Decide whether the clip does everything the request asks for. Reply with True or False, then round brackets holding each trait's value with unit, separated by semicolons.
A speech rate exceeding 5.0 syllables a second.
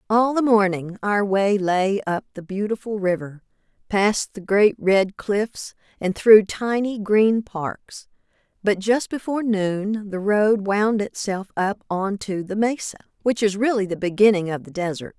False (4.1 syllables/s)